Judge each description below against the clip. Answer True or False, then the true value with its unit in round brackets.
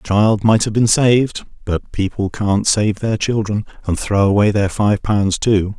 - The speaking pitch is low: True (105 Hz)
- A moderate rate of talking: True (195 wpm)